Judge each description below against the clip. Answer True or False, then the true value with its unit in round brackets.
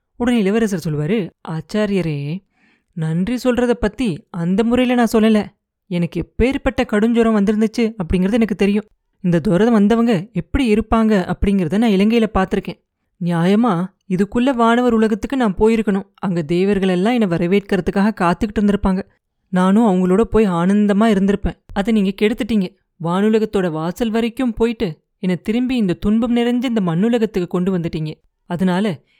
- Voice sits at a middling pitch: False (210 Hz)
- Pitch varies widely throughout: False (3.7 semitones)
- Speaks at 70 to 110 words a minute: False (125 wpm)